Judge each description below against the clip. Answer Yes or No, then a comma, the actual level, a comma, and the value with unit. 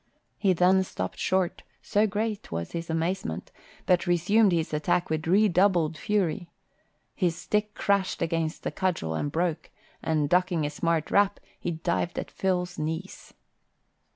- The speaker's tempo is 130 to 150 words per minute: Yes, average, 145 wpm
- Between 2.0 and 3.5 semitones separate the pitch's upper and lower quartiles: Yes, average, 2.9 semitones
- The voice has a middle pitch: Yes, medium, 175 Hz